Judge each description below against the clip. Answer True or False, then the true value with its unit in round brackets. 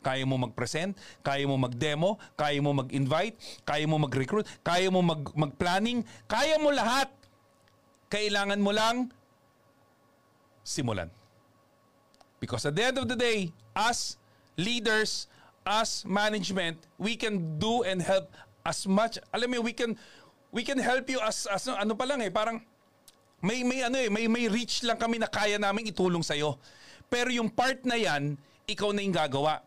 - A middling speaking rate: False (160 wpm)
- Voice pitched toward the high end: True (200 Hz)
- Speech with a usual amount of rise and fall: False (7.0 semitones)